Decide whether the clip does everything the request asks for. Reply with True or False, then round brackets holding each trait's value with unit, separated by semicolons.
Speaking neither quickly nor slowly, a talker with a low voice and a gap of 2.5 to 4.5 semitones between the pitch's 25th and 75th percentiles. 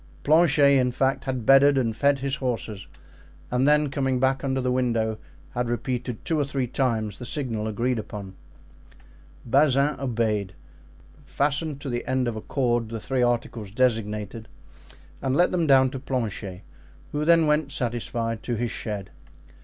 True (160 wpm; 125 Hz; 3.3 semitones)